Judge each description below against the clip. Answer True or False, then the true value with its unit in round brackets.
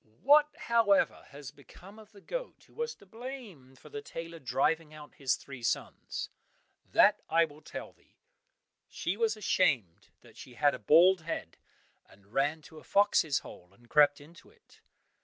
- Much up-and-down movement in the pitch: True (6.9 semitones)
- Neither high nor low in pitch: True (160 Hz)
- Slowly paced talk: False (170 wpm)